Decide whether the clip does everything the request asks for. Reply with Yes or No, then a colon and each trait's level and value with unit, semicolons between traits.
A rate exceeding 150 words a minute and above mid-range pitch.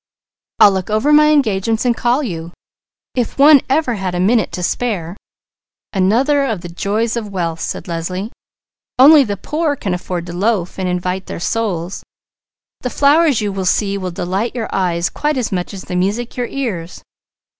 Yes: average, 175 wpm; high, 205 Hz